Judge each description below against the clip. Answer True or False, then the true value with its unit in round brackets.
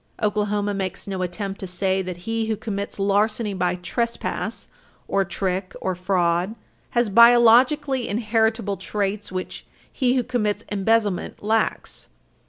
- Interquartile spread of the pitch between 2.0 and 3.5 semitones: True (2.9 semitones)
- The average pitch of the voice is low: False (205 Hz)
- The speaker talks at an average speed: False (130 wpm)